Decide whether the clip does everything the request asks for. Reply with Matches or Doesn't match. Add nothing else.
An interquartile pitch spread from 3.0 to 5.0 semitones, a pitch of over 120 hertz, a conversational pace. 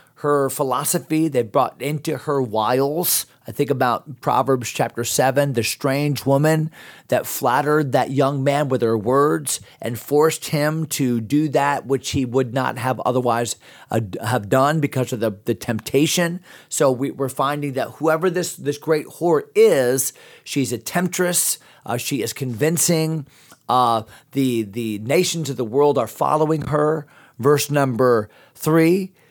Matches